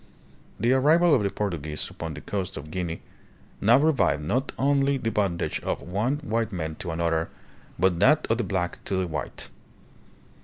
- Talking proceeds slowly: No, average, 165 wpm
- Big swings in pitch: Yes, wide, 7.4 semitones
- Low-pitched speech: Yes, low, 100 Hz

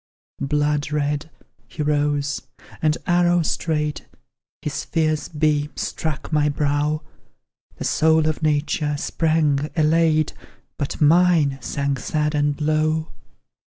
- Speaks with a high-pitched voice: No, medium, 150 Hz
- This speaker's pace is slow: Yes, slow, 110 wpm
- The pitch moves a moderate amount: No, narrow, 1.3 semitones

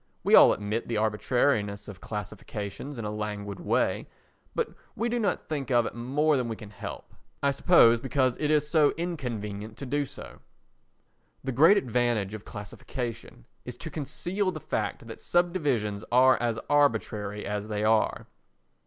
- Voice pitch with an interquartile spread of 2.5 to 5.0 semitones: No, wide, 5.5 semitones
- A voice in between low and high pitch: No, low, 120 Hz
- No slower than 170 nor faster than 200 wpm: No, average, 160 wpm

